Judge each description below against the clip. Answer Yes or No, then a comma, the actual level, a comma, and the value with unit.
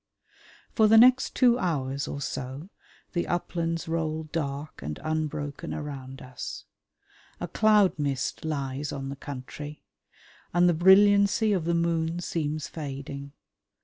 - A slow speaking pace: Yes, slow, 130 wpm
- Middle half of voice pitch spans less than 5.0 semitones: Yes, average, 3.9 semitones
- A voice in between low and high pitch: Yes, medium, 155 Hz